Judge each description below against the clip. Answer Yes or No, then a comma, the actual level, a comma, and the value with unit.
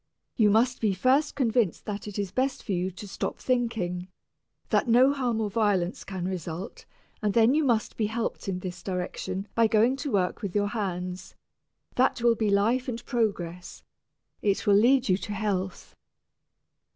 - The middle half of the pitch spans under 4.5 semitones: Yes, average, 4.0 semitones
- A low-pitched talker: No, high, 210 Hz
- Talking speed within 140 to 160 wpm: No, average, 175 wpm